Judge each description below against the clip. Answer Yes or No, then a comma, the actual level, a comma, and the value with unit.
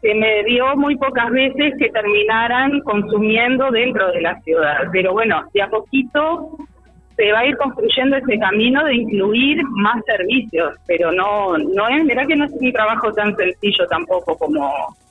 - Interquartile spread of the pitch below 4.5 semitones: No, average, 4.9 semitones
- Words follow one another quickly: No, average, 170 wpm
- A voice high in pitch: Yes, high, 225 Hz